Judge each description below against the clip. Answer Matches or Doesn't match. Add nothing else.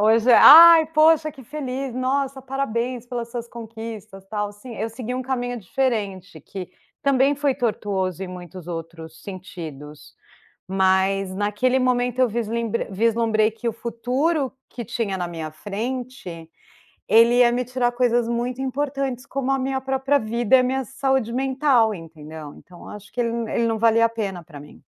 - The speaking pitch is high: Matches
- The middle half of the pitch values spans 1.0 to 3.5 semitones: Doesn't match